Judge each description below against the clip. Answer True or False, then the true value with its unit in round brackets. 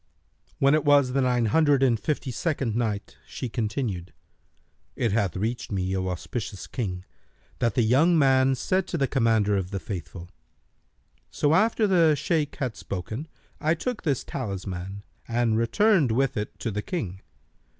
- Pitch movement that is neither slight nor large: False (6.0 semitones)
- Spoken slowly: False (160 wpm)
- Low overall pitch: True (120 Hz)